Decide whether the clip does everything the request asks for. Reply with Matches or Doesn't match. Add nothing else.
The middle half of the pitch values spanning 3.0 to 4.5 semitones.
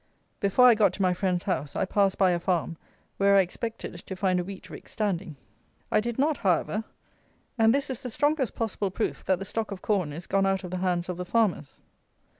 Matches